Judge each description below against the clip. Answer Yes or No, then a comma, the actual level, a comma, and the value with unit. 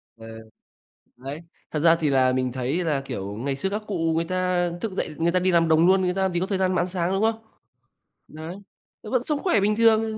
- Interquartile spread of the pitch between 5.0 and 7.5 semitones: No, average, 3.9 semitones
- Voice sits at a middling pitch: Yes, medium, 175 Hz